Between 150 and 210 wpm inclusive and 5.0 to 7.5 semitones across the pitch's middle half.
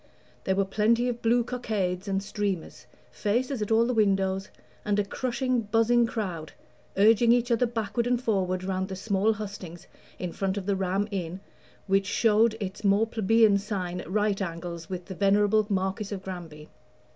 No: average, 170 wpm; average, 2.9 semitones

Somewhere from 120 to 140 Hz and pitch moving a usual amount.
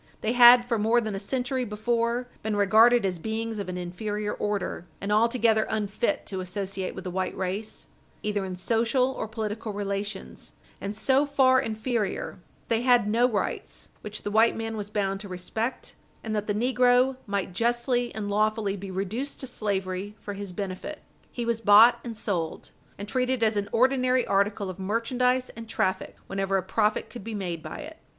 No: high, 215 Hz; average, 3.2 semitones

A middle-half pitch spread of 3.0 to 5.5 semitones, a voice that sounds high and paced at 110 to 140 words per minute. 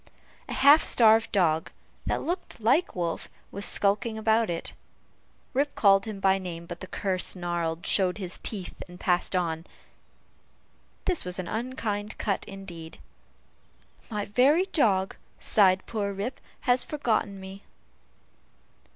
Yes: average, 3.8 semitones; high, 200 Hz; slow, 135 wpm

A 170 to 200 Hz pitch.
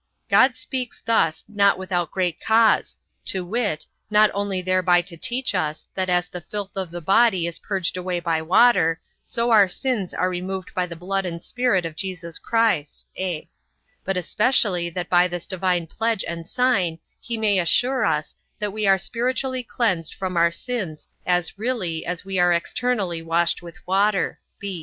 Yes: medium, 185 Hz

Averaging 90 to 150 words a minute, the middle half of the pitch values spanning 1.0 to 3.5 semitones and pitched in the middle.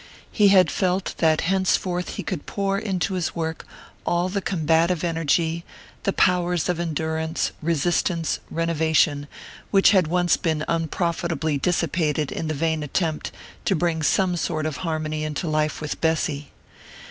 Yes: average, 145 wpm; narrow, 2.4 semitones; medium, 165 Hz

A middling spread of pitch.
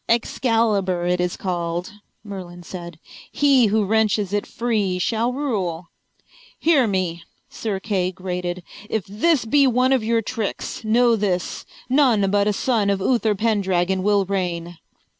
Yes: average, 4.0 semitones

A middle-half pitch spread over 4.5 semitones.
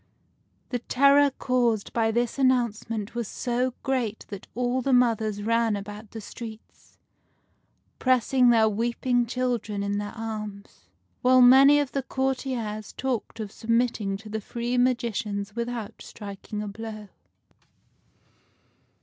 No: average, 2.9 semitones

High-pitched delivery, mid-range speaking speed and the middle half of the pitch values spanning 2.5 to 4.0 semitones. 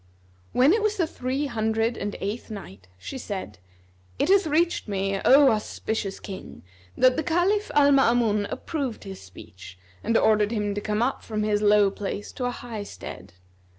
No: high, 220 Hz; average, 175 wpm; average, 5.0 semitones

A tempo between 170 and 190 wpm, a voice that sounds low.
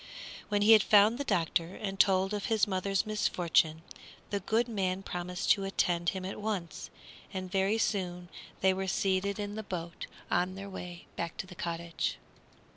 No: average, 175 wpm; high, 190 Hz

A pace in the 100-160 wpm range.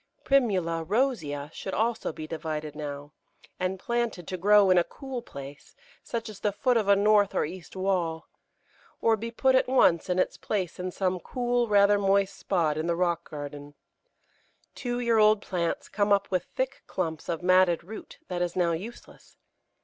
No: average, 180 wpm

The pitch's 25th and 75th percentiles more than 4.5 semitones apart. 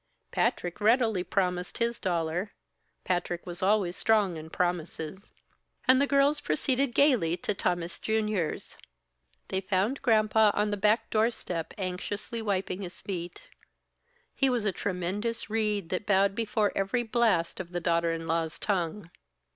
No: average, 3.9 semitones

